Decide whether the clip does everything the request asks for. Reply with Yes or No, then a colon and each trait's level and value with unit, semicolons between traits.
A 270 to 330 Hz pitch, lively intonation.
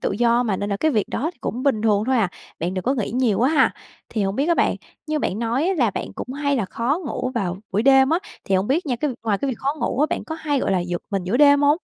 No: high, 245 Hz; wide, 5.7 semitones